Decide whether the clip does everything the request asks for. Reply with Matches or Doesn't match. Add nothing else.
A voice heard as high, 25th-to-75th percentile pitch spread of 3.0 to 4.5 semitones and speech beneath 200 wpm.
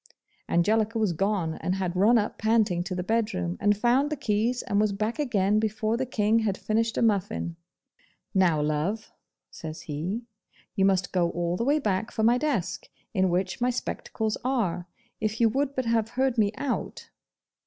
Matches